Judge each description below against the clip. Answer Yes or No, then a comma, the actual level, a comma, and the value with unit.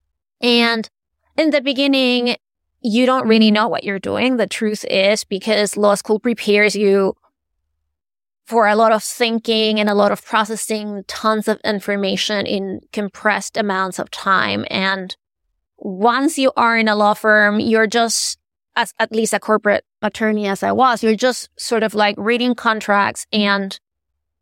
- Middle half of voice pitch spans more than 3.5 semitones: No, narrow, 2.4 semitones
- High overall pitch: Yes, high, 215 Hz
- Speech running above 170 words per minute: No, average, 155 wpm